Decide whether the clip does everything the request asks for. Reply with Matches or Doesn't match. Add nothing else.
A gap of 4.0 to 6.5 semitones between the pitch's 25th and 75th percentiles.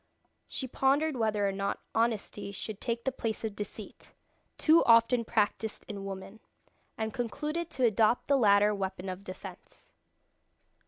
Doesn't match